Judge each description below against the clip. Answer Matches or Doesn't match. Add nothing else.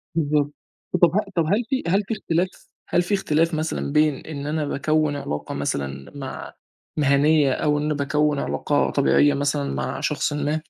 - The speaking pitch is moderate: Matches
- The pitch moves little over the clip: Matches